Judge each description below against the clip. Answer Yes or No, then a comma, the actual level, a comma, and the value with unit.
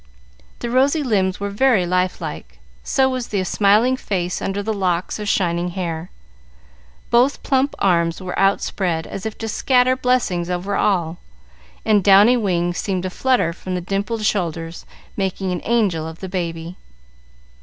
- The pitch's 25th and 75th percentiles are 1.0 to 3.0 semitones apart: No, average, 3.9 semitones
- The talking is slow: No, average, 155 wpm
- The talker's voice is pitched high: Yes, high, 195 Hz